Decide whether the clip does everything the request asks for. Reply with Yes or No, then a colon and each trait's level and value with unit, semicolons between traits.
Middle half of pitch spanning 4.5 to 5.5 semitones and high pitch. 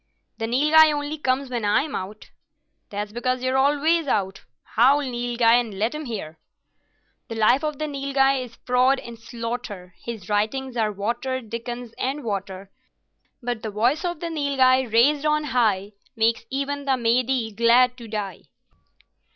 No: average, 3.7 semitones; high, 245 Hz